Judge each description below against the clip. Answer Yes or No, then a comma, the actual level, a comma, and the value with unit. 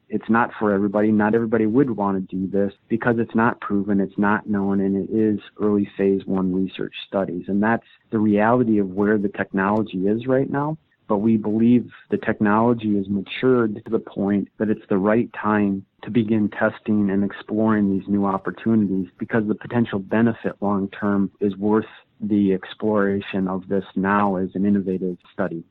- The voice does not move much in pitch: Yes, narrow, 2.0 semitones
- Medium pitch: No, low, 105 Hz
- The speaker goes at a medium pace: Yes, average, 180 wpm